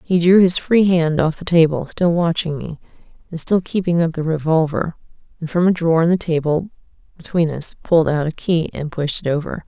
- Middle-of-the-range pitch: Yes, medium, 165 Hz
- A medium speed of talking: No, fast, 210 wpm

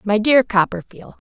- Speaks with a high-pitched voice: Yes, high, 210 Hz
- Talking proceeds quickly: No, average, 140 wpm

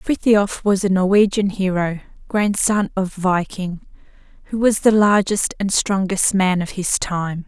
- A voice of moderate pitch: No, high, 195 Hz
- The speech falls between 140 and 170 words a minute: Yes, average, 145 wpm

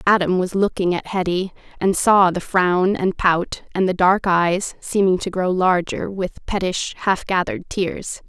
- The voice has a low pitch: No, medium, 185 Hz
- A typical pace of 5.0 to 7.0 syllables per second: No, 4.2 syllables/s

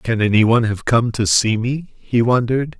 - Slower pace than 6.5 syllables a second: Yes, 4.8 syllables/s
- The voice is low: Yes, low, 115 Hz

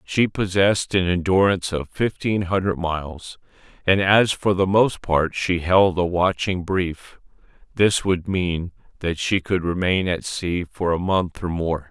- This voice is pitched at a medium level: No, very low, 90 Hz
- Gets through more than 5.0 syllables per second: No, 4.1 syllables/s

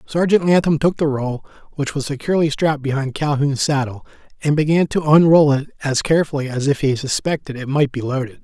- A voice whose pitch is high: No, medium, 145 Hz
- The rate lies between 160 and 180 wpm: No, average, 190 wpm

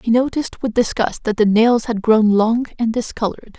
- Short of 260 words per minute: Yes, average, 200 wpm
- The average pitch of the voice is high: Yes, high, 230 Hz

